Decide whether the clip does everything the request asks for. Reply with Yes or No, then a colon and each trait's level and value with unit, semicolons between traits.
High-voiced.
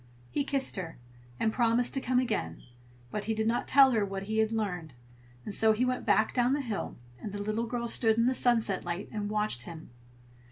Yes: high, 220 Hz